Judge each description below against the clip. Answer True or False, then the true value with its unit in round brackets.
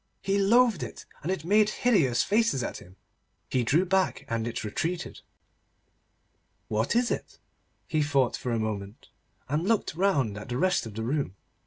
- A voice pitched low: False (150 Hz)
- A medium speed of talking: True (170 wpm)